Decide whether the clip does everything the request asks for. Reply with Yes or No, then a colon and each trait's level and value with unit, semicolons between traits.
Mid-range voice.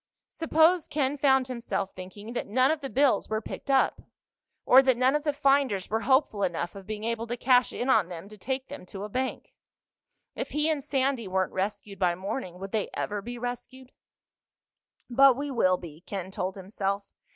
No: high, 240 Hz